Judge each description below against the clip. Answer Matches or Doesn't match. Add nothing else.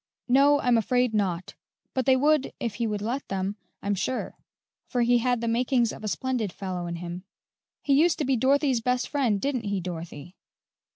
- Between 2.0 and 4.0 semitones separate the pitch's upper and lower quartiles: Doesn't match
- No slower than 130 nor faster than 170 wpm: Doesn't match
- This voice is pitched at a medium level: Doesn't match